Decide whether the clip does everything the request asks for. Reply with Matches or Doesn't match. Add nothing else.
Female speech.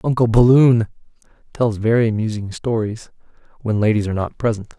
Doesn't match